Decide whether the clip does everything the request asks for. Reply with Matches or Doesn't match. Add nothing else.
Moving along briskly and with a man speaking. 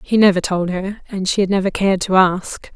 Doesn't match